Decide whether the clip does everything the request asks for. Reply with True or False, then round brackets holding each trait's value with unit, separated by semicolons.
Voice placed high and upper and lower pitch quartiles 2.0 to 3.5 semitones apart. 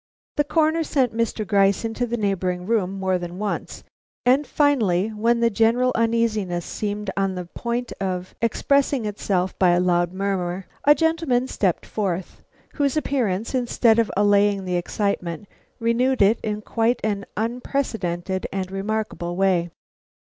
False (210 Hz; 4.0 semitones)